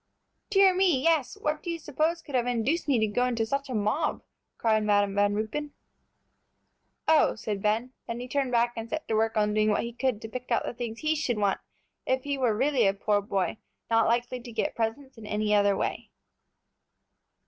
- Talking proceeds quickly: Yes, fast, 210 wpm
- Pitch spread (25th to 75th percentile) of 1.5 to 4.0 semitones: No, average, 4.5 semitones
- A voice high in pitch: Yes, high, 235 Hz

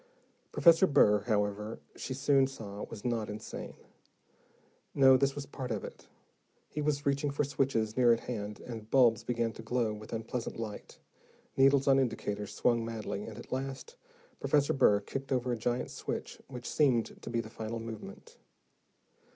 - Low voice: Yes, low, 120 Hz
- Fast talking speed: No, average, 165 wpm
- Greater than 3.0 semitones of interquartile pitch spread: Yes, average, 3.6 semitones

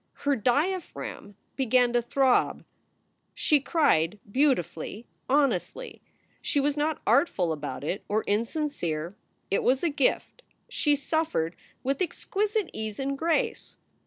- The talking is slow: Yes, slow, 120 wpm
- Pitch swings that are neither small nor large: No, wide, 6.6 semitones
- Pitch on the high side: Yes, very high, 270 Hz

